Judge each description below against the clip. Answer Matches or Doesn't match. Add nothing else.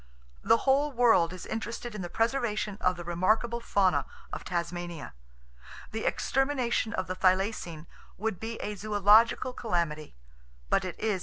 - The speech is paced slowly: Doesn't match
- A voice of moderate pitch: Doesn't match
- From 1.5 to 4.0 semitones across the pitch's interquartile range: Doesn't match